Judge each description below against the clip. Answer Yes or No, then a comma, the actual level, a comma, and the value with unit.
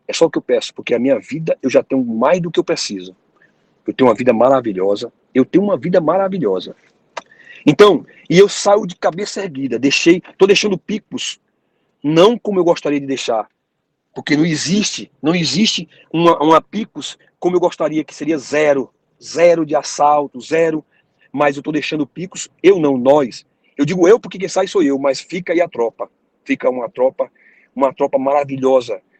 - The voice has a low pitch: No, medium, 165 Hz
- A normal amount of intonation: No, wide, 5.8 semitones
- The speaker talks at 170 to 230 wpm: Yes, fast, 185 wpm